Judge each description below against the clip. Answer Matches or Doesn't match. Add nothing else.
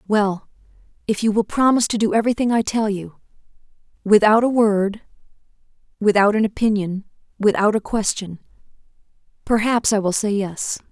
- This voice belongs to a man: Doesn't match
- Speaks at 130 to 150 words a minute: Matches